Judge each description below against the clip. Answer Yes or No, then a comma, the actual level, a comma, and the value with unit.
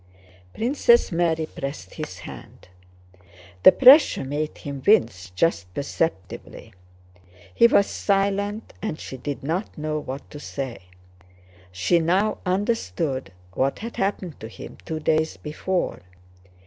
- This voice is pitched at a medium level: Yes, medium, 160 Hz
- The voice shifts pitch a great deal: Yes, wide, 6.5 semitones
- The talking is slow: Yes, slow, 120 wpm